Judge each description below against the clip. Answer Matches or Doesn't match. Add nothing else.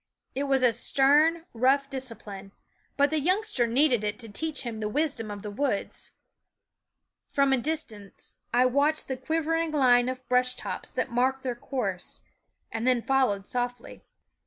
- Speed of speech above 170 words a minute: Doesn't match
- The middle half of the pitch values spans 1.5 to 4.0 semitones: Matches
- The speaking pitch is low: Doesn't match